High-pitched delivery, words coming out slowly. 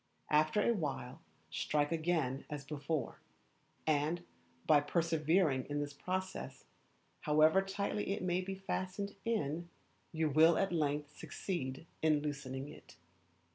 No: medium, 155 Hz; slow, 125 wpm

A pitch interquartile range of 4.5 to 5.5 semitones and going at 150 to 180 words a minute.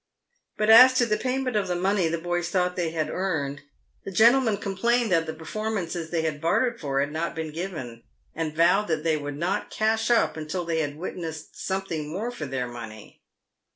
No: average, 4.9 semitones; average, 200 wpm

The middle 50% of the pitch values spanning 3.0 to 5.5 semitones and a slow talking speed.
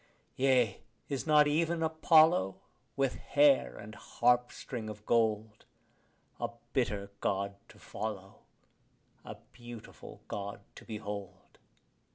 Yes: average, 5.2 semitones; slow, 105 wpm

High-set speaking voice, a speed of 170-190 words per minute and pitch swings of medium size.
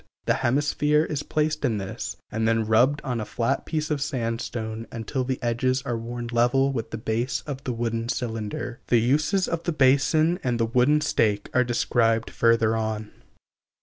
No: low, 120 Hz; average, 180 wpm; average, 3.6 semitones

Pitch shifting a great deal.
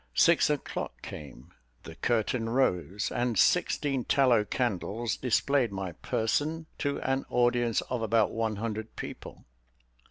No: average, 3.6 semitones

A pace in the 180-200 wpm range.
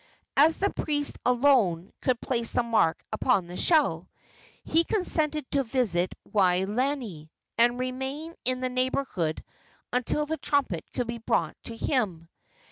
No: slow, 135 wpm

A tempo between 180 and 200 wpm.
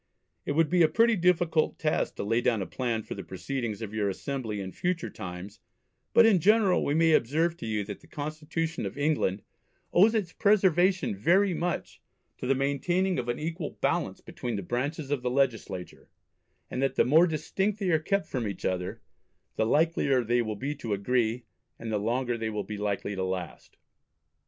Yes: average, 195 wpm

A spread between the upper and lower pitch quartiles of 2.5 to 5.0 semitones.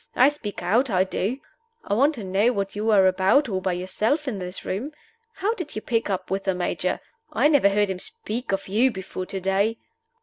Yes: average, 4.6 semitones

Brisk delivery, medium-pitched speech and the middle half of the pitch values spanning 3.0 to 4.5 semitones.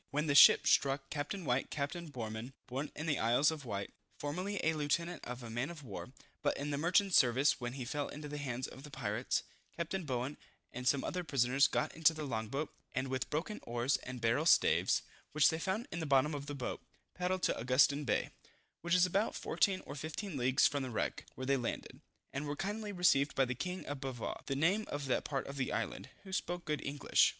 Yes: fast, 220 wpm; medium, 145 Hz; average, 4.0 semitones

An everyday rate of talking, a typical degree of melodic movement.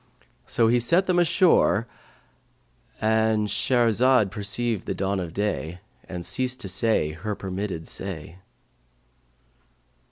No: slow, 115 wpm; average, 4.2 semitones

